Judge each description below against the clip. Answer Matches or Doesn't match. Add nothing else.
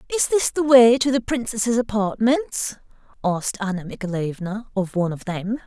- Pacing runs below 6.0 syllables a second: Matches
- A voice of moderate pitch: Doesn't match